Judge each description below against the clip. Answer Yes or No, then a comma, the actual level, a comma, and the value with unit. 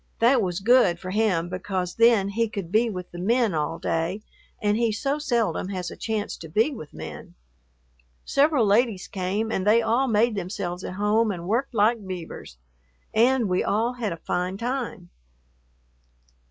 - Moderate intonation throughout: Yes, average, 4.2 semitones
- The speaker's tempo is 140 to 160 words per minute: No, average, 170 wpm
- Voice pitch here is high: Yes, high, 210 Hz